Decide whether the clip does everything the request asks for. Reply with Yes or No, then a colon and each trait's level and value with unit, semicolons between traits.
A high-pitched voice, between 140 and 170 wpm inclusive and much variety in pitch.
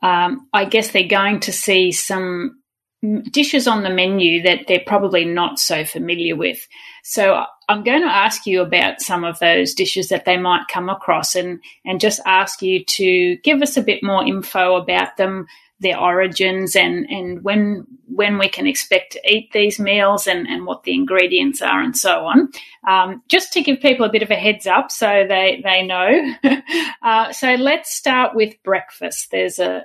No: high, 200 Hz; average, 190 wpm; wide, 6.1 semitones